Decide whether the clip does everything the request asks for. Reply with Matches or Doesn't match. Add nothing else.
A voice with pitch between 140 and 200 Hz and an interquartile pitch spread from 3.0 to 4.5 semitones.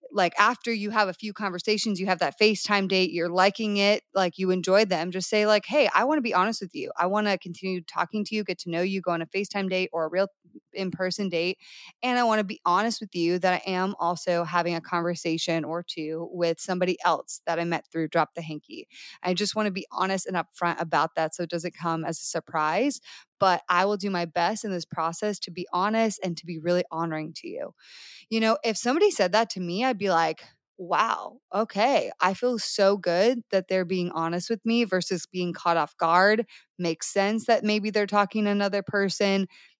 Matches